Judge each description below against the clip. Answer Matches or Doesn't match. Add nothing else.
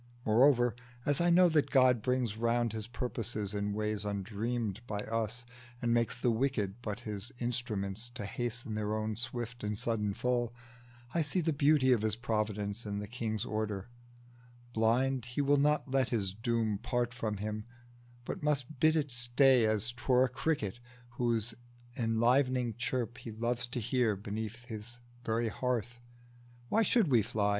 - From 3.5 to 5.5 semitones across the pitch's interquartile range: Doesn't match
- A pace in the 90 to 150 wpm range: Doesn't match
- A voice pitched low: Matches